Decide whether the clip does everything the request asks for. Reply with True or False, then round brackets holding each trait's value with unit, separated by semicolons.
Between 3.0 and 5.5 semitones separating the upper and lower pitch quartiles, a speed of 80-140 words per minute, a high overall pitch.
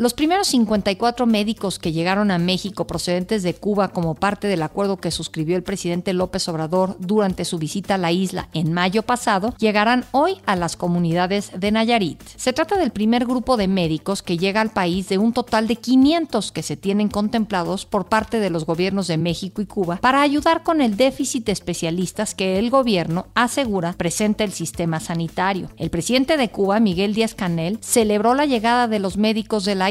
False (4.3 semitones; 190 wpm; 200 Hz)